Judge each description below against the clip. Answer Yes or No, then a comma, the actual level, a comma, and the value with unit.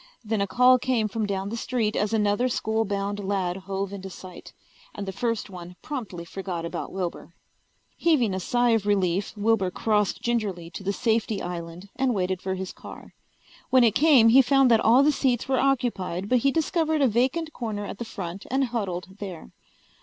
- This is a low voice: No, high, 210 Hz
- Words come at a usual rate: Yes, average, 190 wpm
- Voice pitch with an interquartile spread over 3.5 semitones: Yes, average, 4.3 semitones